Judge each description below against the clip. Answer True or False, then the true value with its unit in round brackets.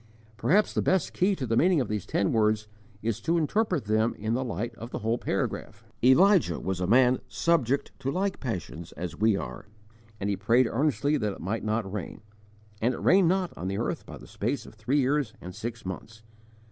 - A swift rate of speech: True (210 wpm)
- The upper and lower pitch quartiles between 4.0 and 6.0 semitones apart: True (5.4 semitones)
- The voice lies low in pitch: True (115 Hz)